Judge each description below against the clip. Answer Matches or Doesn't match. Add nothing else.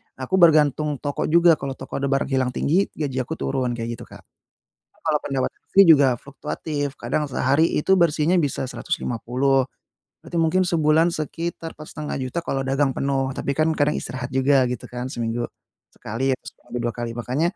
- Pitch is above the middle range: Doesn't match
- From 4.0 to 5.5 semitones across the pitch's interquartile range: Doesn't match